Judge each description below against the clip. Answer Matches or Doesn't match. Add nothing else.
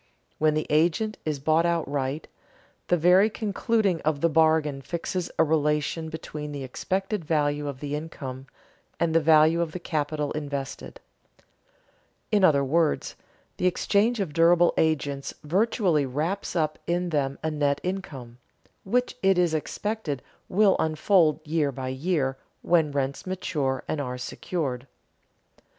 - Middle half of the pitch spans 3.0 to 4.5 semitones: Matches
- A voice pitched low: Doesn't match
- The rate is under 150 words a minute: Matches